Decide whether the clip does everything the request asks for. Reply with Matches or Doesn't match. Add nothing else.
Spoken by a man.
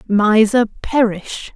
Doesn't match